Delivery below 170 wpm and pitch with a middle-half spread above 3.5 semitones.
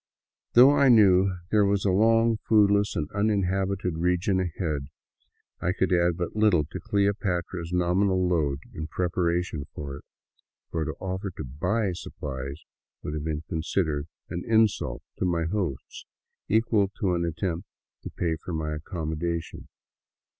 Yes: average, 155 wpm; average, 3.9 semitones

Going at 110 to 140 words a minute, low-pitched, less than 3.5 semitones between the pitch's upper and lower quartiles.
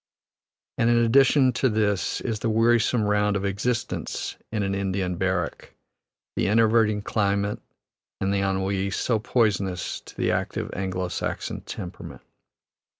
Yes: slow, 135 wpm; low, 105 Hz; average, 2.8 semitones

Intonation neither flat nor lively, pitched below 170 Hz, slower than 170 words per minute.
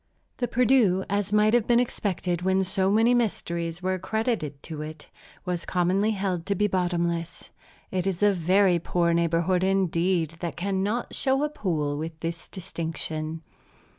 No: average, 3.4 semitones; medium, 185 Hz; average, 155 wpm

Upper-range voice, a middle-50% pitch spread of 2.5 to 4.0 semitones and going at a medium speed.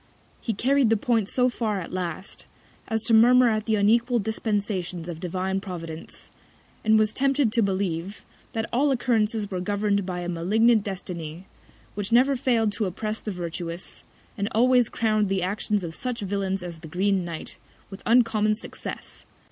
Yes: high, 205 Hz; average, 3.7 semitones; average, 165 wpm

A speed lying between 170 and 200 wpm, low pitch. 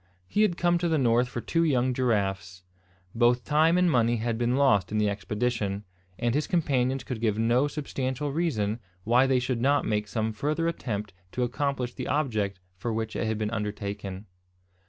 Yes: average, 185 wpm; low, 120 Hz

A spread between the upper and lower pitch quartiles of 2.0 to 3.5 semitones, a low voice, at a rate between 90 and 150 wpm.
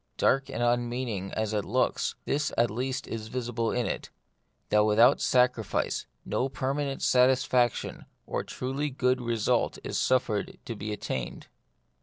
Yes: average, 2.8 semitones; low, 120 Hz; average, 140 wpm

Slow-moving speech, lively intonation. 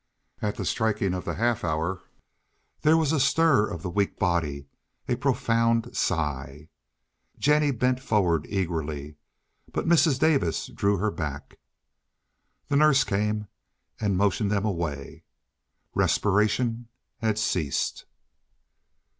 Yes: slow, 115 wpm; wide, 6.3 semitones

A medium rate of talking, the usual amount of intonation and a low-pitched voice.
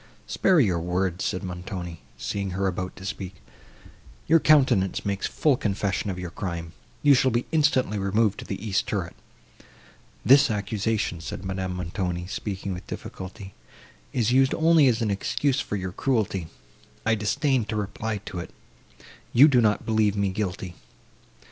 Yes: average, 155 wpm; average, 4.1 semitones; low, 100 Hz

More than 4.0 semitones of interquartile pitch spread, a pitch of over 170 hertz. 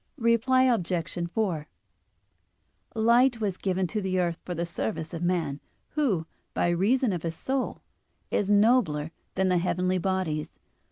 Yes: average, 4.6 semitones; medium, 185 Hz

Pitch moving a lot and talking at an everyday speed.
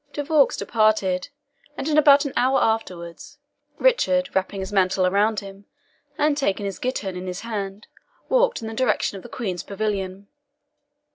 Yes: wide, 6.0 semitones; average, 160 wpm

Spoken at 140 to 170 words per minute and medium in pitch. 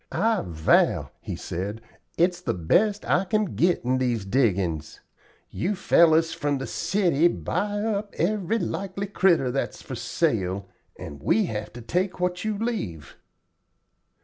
Yes: average, 145 wpm; medium, 170 Hz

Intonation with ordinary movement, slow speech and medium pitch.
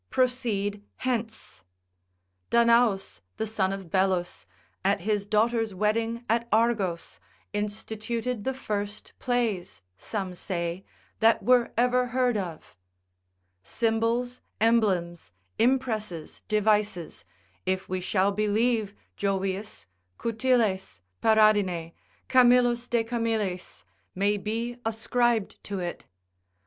No: average, 3.3 semitones; slow, 95 wpm; high, 215 Hz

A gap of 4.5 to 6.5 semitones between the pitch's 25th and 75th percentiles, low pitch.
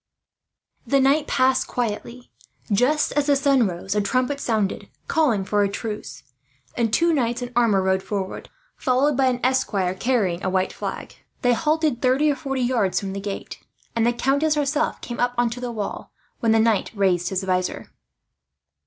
No: average, 5.1 semitones; high, 240 Hz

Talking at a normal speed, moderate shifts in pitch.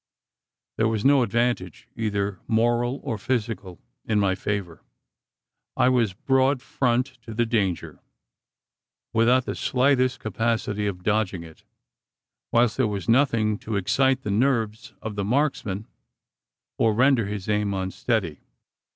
No: slow, 130 wpm; average, 3.5 semitones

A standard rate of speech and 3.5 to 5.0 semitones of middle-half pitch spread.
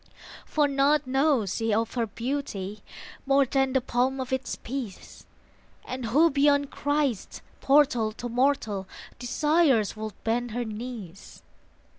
No: slow, 130 wpm; average, 3.8 semitones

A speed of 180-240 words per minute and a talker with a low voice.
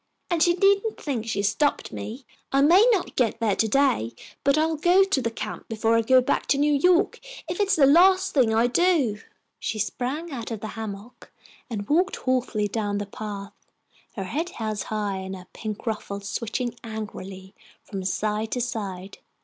No: average, 190 wpm; high, 230 Hz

